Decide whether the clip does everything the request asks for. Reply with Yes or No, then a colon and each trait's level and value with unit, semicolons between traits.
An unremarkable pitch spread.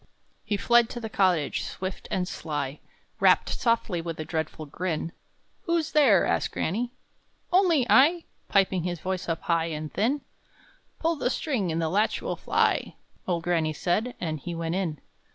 No: wide, 6.4 semitones